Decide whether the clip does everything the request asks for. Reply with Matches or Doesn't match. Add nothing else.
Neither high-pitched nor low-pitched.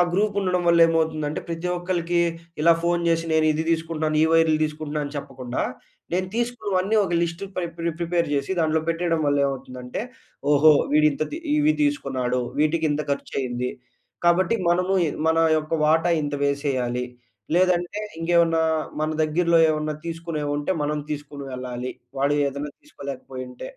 Matches